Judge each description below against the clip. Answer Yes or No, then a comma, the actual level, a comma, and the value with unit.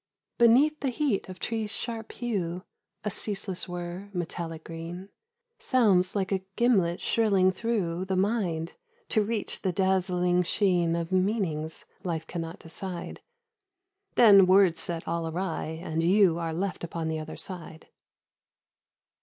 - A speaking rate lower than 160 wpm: Yes, average, 140 wpm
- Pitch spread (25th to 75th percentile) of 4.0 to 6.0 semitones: No, average, 3.4 semitones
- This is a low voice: No, medium, 185 Hz